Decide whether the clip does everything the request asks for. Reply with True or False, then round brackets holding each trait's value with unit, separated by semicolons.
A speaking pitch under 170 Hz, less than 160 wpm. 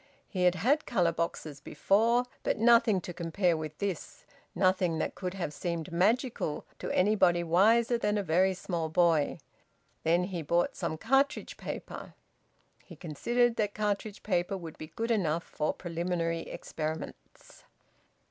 False (180 Hz; 145 wpm)